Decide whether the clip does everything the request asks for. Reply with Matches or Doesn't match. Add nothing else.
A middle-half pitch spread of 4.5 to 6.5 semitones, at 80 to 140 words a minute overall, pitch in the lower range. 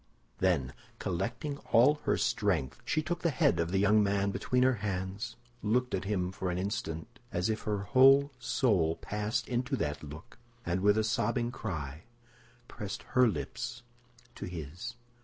Doesn't match